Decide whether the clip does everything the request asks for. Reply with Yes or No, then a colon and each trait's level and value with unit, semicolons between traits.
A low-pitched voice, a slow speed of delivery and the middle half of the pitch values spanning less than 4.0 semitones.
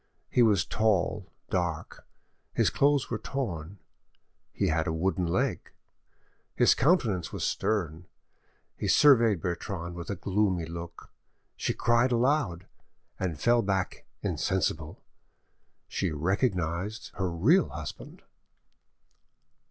No: very low, 95 Hz; slow, 110 wpm; wide, 5.4 semitones